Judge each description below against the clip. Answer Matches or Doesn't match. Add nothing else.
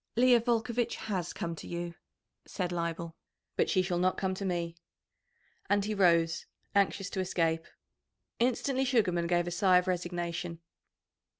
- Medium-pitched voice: Matches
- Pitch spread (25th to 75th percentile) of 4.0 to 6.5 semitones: Doesn't match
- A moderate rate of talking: Matches